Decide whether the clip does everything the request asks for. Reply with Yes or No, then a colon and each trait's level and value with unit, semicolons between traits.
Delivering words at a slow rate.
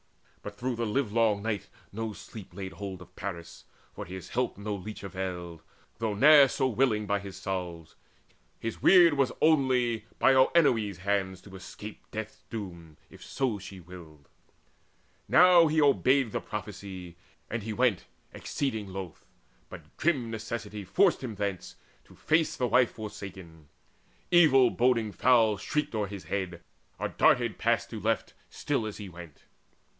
No: average, 150 wpm